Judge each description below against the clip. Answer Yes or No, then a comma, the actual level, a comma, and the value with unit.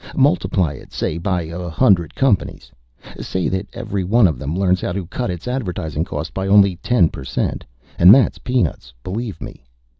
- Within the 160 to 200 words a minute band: Yes, average, 180 wpm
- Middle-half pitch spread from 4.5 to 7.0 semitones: No, average, 3.8 semitones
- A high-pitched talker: No, very low, 95 Hz